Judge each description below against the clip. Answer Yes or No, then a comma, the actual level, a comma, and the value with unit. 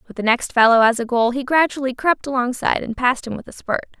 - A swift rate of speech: Yes, fast, 255 wpm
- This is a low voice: No, very high, 250 Hz